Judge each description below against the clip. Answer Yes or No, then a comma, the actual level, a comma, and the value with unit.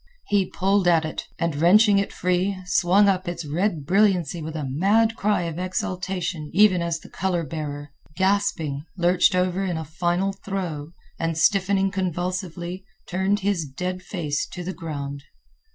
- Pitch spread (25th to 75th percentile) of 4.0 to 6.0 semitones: No, average, 3.1 semitones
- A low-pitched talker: No, medium, 180 Hz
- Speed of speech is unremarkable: Yes, average, 155 wpm